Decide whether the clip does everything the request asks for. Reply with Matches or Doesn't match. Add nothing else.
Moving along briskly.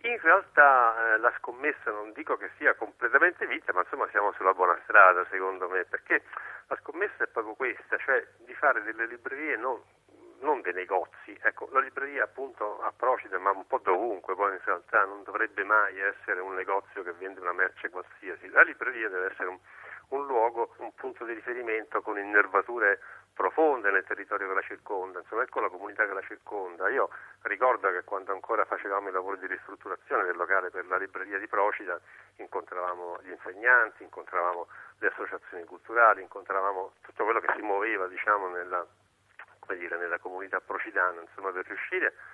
Matches